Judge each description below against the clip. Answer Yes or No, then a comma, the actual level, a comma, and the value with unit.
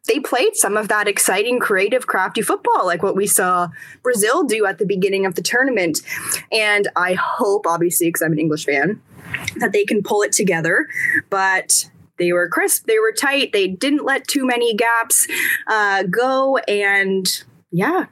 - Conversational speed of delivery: Yes, average, 175 wpm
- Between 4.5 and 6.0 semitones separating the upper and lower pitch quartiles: Yes, wide, 5.5 semitones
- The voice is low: No, high, 205 Hz